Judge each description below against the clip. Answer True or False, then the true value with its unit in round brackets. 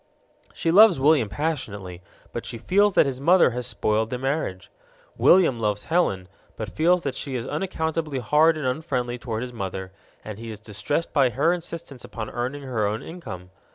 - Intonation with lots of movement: True (6.6 semitones)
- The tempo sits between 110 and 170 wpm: False (180 wpm)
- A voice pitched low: True (130 Hz)